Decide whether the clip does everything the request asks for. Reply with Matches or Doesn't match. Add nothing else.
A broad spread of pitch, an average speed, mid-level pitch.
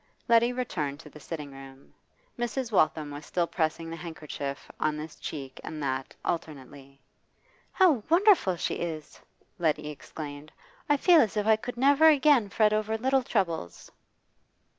Matches